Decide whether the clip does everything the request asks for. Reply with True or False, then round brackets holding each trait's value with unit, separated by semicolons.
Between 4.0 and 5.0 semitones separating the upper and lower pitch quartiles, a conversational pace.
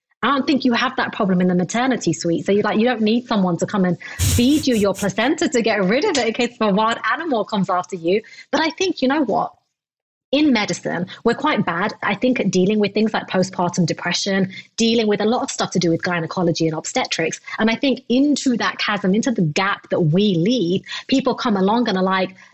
False (4.7 semitones; 235 wpm)